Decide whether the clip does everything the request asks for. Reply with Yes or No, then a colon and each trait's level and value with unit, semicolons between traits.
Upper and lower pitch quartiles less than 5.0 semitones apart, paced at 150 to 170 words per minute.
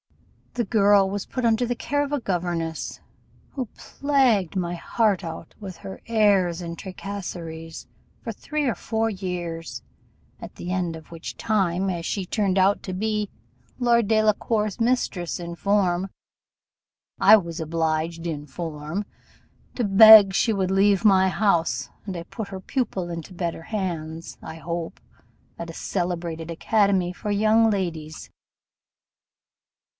No: average, 4.1 semitones; average, 140 wpm